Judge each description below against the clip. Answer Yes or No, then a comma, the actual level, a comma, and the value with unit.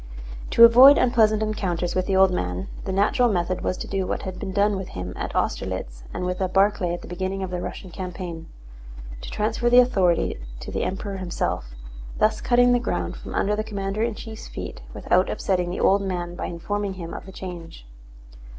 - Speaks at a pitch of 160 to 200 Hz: Yes, high, 190 Hz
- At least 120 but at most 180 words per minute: No, average, 195 wpm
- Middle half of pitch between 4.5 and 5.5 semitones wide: No, average, 3.1 semitones